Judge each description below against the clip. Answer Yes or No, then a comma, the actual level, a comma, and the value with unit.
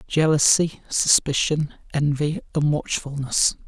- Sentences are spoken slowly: Yes, slow, 80 wpm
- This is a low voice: No, medium, 145 Hz